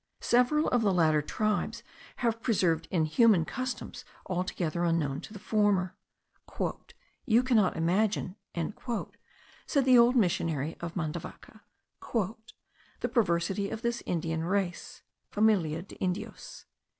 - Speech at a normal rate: No, slow, 115 wpm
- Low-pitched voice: No, high, 190 Hz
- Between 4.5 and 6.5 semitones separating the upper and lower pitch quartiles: Yes, average, 5.1 semitones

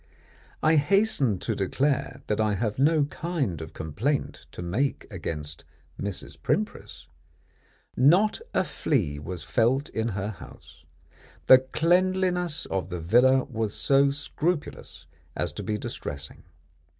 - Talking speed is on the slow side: Yes, slow, 125 wpm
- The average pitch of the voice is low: Yes, low, 125 Hz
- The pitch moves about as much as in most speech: No, wide, 7.5 semitones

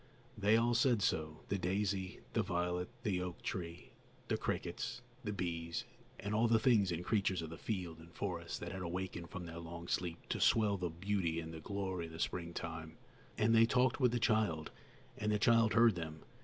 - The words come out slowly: No, average, 195 wpm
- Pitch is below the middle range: Yes, very low, 90 Hz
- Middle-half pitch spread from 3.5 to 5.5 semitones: Yes, average, 4.0 semitones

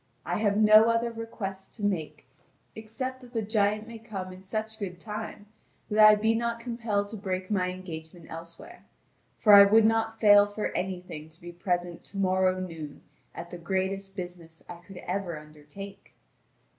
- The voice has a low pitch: No, high, 195 Hz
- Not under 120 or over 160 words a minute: No, average, 170 wpm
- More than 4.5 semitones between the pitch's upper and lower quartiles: No, average, 3.4 semitones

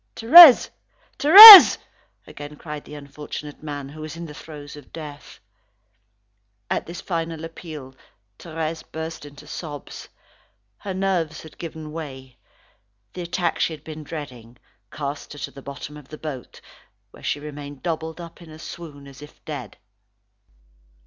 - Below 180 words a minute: Yes, average, 150 wpm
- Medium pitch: Yes, medium, 155 Hz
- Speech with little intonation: Yes, narrow, 2.3 semitones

